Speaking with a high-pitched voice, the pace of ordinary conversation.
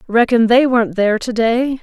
Yes: high, 235 Hz; average, 165 wpm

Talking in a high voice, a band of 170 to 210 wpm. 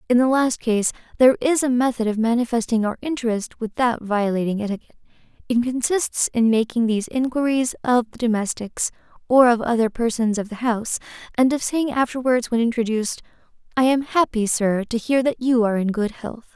Yes: high, 235 Hz; average, 180 wpm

